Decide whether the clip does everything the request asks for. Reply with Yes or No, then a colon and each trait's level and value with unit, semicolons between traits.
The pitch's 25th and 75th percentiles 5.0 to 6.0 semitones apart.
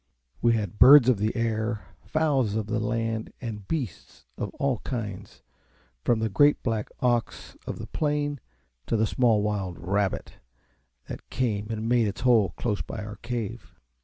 No: average, 2.8 semitones